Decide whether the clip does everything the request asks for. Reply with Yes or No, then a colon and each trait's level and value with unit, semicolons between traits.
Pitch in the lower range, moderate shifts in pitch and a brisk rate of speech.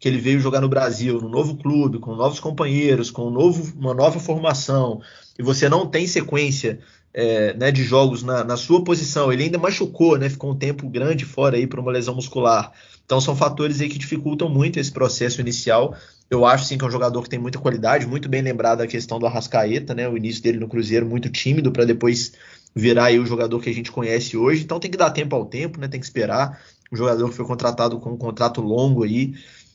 Yes: low, 130 Hz; average, 3.2 semitones; fast, 230 wpm